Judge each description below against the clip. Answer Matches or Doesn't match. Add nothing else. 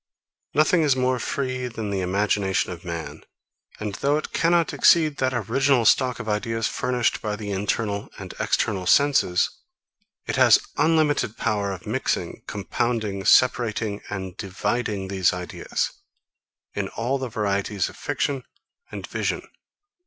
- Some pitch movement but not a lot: Matches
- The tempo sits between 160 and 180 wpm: Doesn't match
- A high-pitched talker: Doesn't match